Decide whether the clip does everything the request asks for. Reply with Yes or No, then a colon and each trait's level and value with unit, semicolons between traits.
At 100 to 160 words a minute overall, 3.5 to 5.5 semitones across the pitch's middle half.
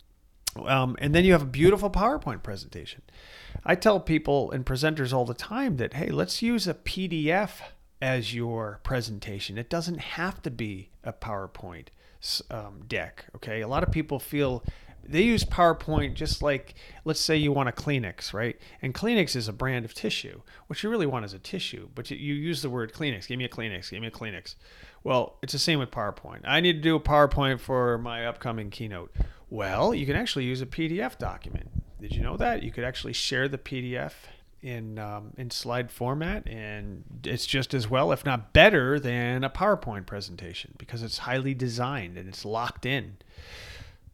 No: average, 190 wpm; average, 5.0 semitones